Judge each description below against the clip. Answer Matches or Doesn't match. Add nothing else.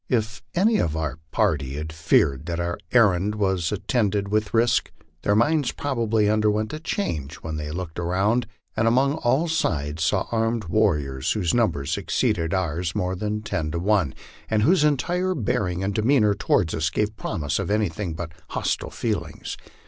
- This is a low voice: Matches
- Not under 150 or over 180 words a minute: Matches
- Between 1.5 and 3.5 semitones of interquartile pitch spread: Doesn't match